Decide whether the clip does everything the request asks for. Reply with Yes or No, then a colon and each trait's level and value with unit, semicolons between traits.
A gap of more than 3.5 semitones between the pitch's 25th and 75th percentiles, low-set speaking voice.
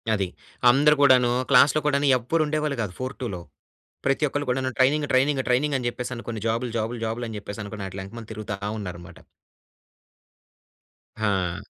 Yes: average, 4.6 semitones; low, 120 Hz